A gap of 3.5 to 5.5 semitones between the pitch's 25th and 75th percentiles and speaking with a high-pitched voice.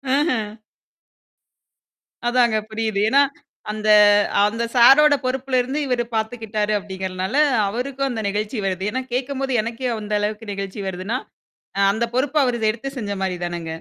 Yes: average, 4.0 semitones; high, 225 Hz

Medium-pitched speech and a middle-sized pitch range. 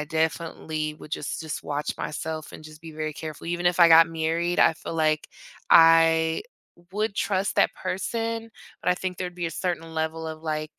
No: medium, 160 Hz; narrow, 2.0 semitones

